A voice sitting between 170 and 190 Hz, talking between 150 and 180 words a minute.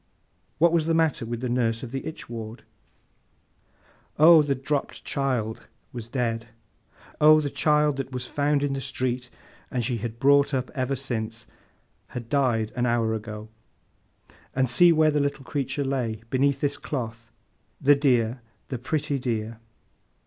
No: low, 130 Hz; average, 155 wpm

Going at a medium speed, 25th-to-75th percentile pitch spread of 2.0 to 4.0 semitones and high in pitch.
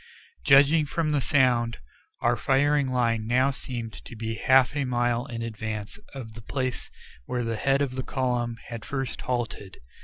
No: average, 165 wpm; narrow, 2.6 semitones; low, 125 Hz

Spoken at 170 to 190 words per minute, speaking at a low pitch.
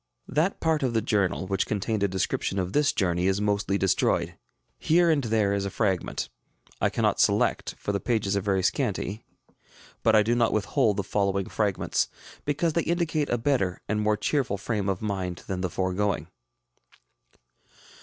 Yes: average, 175 wpm; low, 105 Hz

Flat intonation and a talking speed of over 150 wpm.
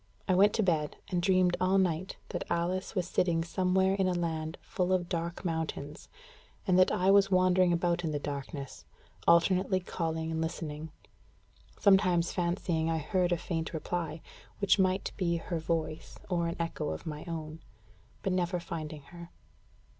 Yes: narrow, 2.3 semitones; average, 165 wpm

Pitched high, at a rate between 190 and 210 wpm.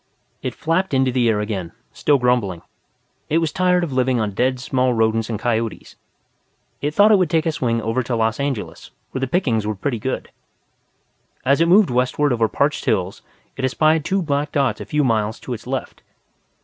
No: low, 130 Hz; average, 195 wpm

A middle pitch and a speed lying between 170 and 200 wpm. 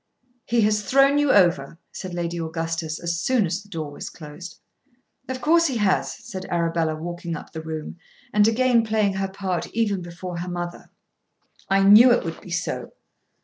Yes: medium, 180 Hz; average, 180 wpm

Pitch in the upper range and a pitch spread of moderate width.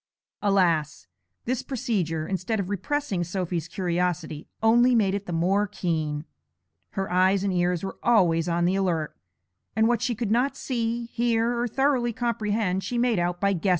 Yes: high, 195 Hz; average, 4.9 semitones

